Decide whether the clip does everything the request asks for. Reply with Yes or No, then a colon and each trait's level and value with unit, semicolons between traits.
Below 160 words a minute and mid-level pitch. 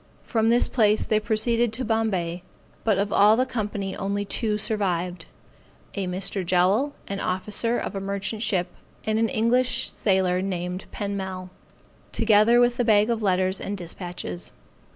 No: average, 150 wpm; high, 205 Hz